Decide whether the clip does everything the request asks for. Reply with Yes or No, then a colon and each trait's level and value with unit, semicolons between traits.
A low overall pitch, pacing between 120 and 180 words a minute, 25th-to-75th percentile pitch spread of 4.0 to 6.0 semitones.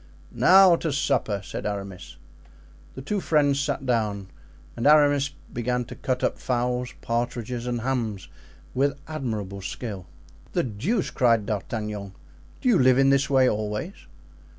Yes: low, 125 Hz; average, 140 wpm; average, 4.7 semitones